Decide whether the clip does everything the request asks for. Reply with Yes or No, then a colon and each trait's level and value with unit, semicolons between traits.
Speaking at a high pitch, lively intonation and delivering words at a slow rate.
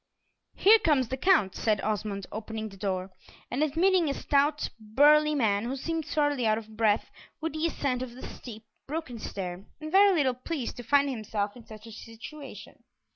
No: very high, 255 Hz; wide, 5.8 semitones; average, 180 wpm